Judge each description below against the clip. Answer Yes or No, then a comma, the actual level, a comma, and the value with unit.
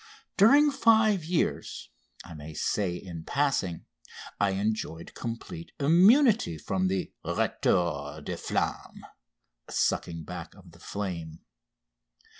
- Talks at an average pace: No, slow, 110 wpm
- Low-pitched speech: Yes, low, 100 Hz